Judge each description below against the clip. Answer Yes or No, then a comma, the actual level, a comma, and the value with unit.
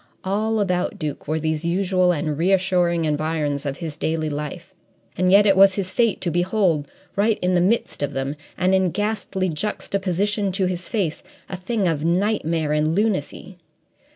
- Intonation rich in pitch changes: No, average, 3.8 semitones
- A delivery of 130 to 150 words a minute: No, average, 170 wpm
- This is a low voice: No, medium, 180 Hz